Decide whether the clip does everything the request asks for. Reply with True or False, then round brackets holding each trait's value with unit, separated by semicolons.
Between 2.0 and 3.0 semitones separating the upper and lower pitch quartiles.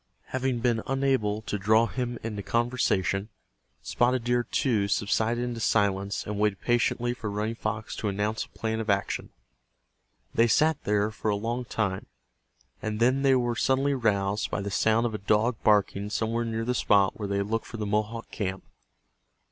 True (2.7 semitones)